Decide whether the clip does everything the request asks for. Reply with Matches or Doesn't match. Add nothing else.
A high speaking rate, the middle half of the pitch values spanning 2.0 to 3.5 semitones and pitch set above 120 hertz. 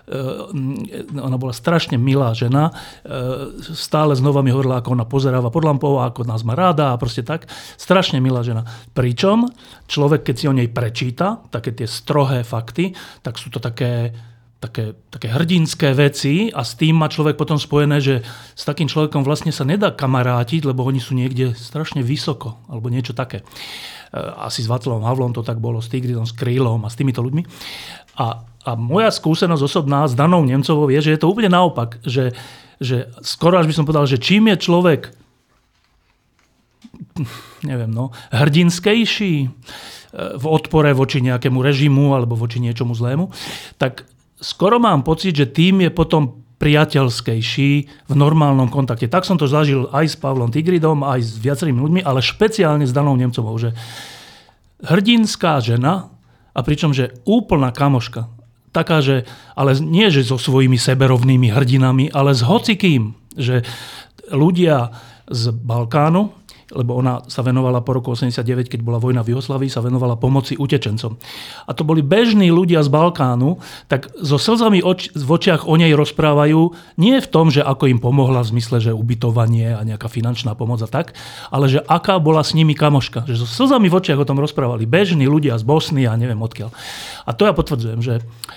Doesn't match